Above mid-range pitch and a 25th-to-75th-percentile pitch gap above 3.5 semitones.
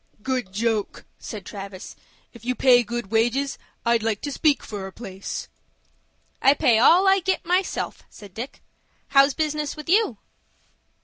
Yes: high, 245 Hz; average, 5.2 semitones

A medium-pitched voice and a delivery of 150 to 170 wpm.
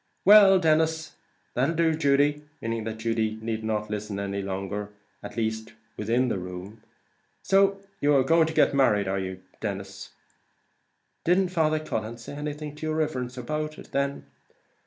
No: low, 130 Hz; average, 155 wpm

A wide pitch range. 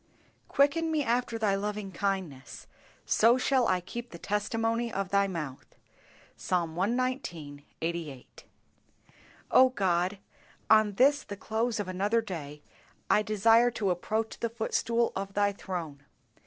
No: average, 4.3 semitones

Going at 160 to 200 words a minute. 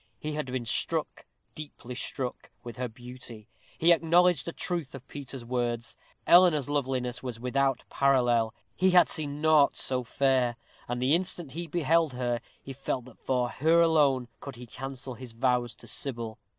Yes: average, 165 wpm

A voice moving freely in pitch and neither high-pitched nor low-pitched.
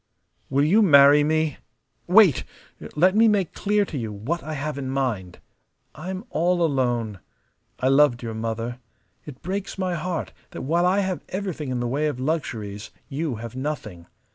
Yes: wide, 6.4 semitones; medium, 150 Hz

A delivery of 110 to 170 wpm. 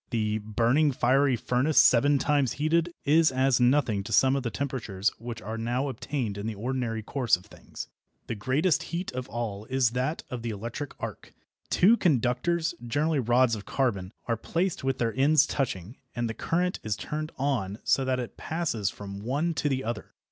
No: average, 185 wpm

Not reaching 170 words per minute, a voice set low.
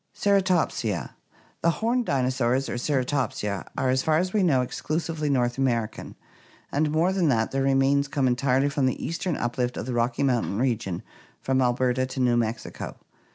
No: average, 175 wpm; low, 130 Hz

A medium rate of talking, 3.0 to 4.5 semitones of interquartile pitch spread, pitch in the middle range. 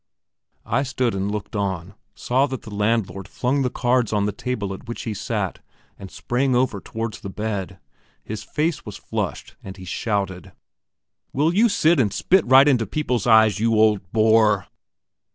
No: average, 170 wpm; average, 4.0 semitones; low, 110 Hz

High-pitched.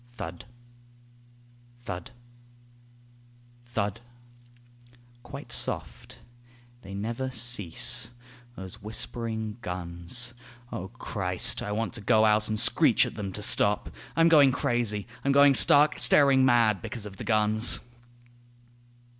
No: low, 110 Hz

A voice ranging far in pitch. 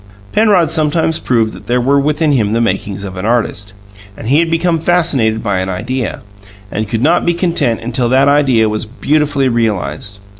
Yes: wide, 5.8 semitones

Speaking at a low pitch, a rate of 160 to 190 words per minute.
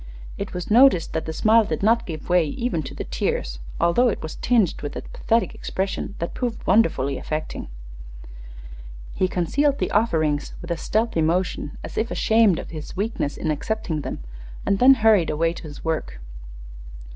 No: medium, 180 Hz; average, 175 wpm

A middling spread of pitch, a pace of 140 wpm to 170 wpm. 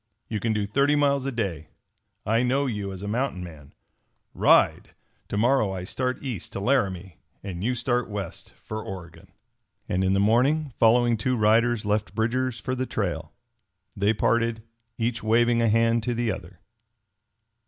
Yes: average, 3.8 semitones; average, 165 wpm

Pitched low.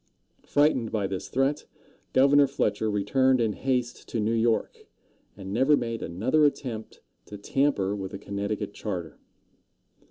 Yes: low, 115 Hz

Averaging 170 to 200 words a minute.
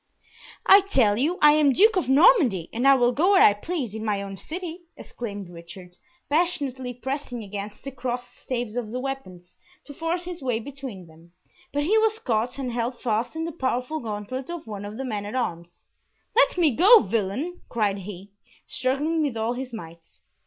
Yes: average, 190 wpm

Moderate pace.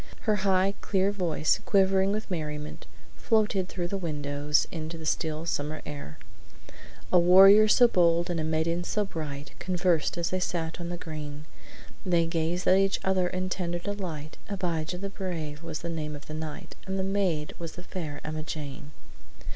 Yes: average, 170 wpm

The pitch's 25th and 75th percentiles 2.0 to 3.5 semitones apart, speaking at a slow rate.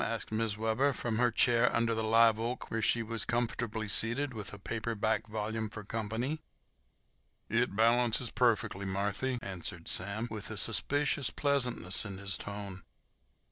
No: narrow, 2.4 semitones; average, 155 wpm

